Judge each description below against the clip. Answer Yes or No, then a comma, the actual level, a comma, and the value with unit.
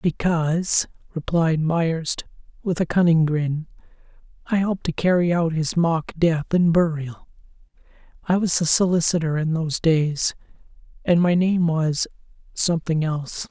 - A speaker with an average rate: No, slow, 125 wpm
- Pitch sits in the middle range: Yes, medium, 165 Hz